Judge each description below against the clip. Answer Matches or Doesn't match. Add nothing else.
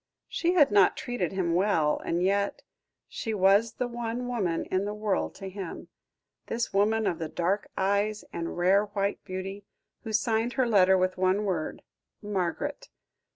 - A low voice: Doesn't match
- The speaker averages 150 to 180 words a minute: Matches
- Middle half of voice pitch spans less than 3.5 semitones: Matches